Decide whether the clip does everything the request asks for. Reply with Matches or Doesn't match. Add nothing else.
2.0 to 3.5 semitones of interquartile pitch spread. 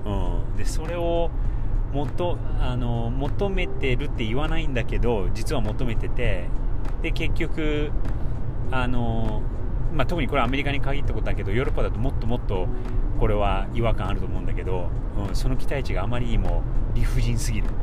Matches